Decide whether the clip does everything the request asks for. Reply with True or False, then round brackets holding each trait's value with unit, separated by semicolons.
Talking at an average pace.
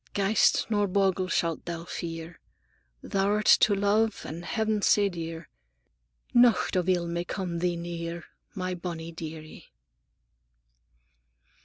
False (125 wpm)